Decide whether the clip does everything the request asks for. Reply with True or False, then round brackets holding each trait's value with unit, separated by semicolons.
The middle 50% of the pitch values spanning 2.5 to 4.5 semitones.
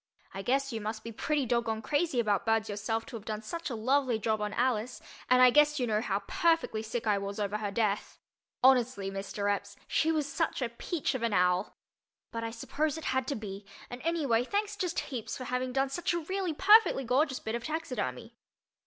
False (4.9 semitones)